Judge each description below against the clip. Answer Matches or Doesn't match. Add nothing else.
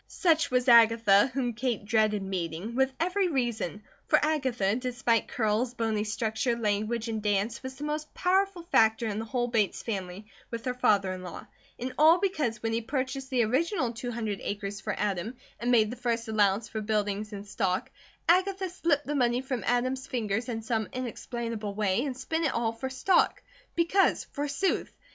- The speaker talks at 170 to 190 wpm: Matches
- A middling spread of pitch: Matches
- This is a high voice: Matches